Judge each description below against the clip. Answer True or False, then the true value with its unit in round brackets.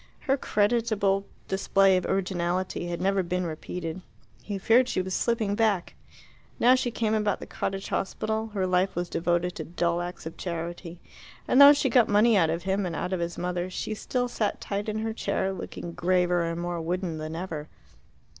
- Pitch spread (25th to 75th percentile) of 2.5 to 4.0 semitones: True (3.4 semitones)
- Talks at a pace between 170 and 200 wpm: True (190 wpm)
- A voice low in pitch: False (185 Hz)